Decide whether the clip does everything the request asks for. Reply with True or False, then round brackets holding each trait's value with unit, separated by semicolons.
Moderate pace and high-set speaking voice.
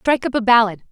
False (265 wpm; 230 Hz)